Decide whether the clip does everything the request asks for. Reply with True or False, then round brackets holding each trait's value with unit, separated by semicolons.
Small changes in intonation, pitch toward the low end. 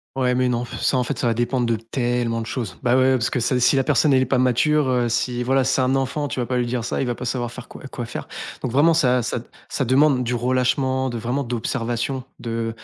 True (1.6 semitones; 125 Hz)